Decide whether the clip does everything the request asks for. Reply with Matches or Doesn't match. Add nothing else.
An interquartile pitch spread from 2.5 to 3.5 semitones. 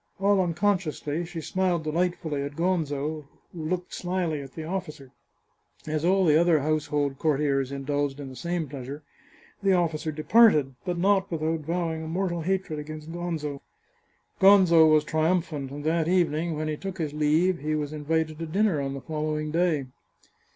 Matches